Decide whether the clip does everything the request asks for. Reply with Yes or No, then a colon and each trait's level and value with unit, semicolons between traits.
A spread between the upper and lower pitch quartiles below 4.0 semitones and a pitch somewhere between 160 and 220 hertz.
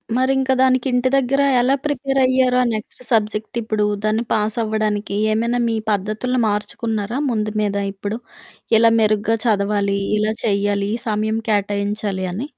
Yes: average, 2.9 semitones; high, 215 Hz